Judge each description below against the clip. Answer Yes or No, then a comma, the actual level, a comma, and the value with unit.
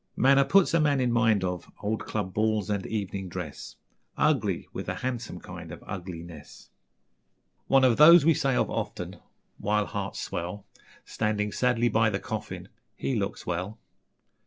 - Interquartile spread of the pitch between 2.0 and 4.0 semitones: No, average, 5.2 semitones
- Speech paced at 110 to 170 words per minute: Yes, average, 160 wpm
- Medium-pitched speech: No, low, 105 Hz